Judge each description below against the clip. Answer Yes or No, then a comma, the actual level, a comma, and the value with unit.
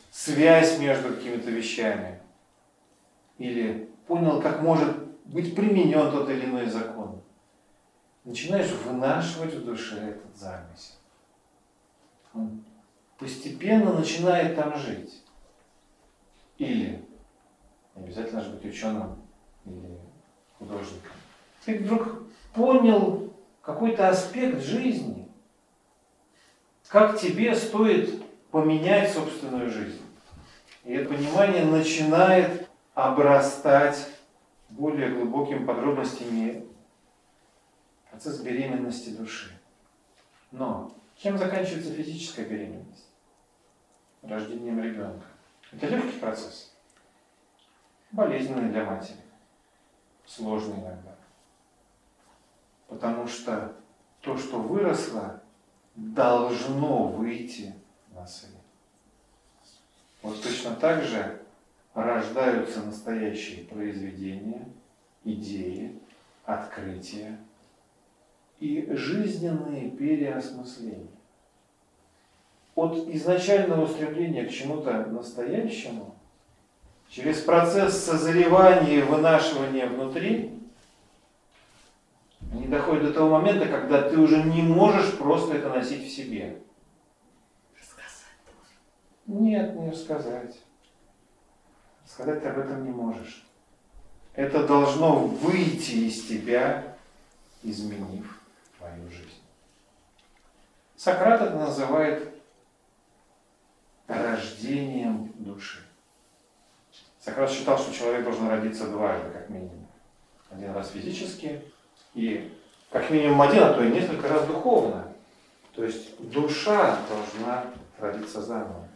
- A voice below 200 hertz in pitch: Yes, low, 135 Hz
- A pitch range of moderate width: No, wide, 6.8 semitones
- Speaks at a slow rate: Yes, slow, 85 wpm